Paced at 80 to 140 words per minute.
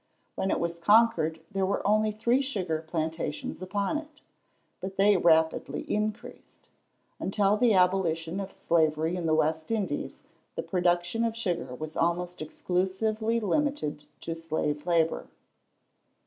Yes: slow, 135 wpm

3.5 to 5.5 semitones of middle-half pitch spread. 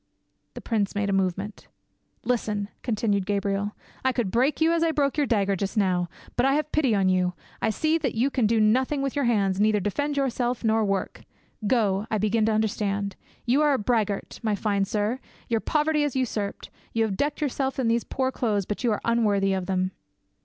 Yes: average, 4.5 semitones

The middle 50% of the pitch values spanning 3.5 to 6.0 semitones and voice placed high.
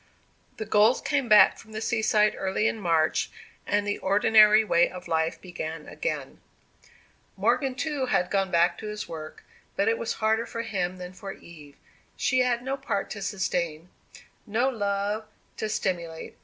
Yes: average, 3.9 semitones; high, 205 Hz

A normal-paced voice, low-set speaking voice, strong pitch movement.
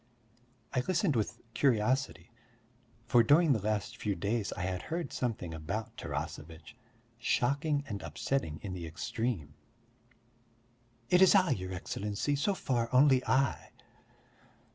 No: slow, 120 wpm; low, 120 Hz; wide, 6.2 semitones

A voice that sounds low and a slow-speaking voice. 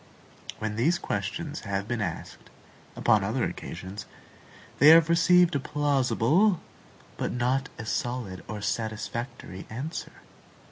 Yes: low, 120 Hz; slow, 120 wpm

